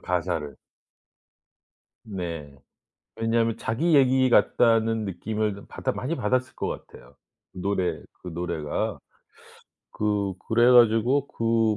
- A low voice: Yes, low, 110 Hz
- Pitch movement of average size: Yes, average, 4.4 semitones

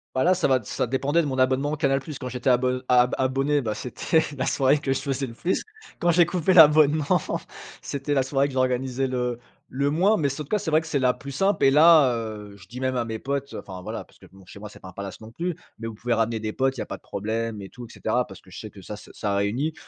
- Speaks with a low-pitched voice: Yes, low, 130 Hz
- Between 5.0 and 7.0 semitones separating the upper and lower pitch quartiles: No, average, 3.9 semitones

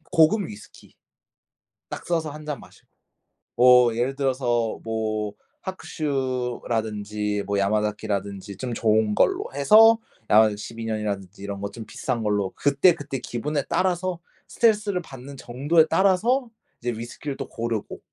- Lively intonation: Yes, wide, 6.2 semitones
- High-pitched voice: No, low, 120 Hz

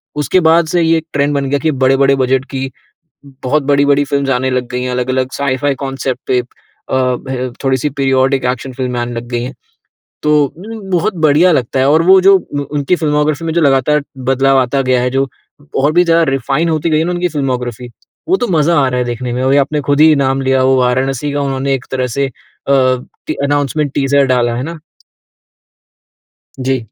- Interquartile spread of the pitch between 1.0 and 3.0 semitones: Yes, narrow, 2.5 semitones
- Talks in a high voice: No, low, 135 Hz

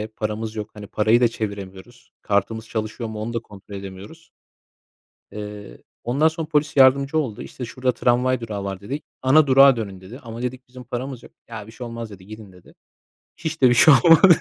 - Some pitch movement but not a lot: Yes, average, 3.8 semitones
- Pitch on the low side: Yes, low, 115 Hz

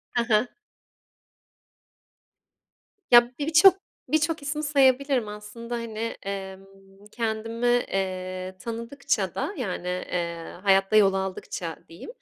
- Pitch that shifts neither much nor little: Yes, average, 4.6 semitones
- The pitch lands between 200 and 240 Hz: Yes, high, 225 Hz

